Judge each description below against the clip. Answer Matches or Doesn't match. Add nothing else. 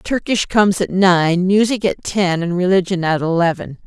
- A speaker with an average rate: Matches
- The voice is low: Doesn't match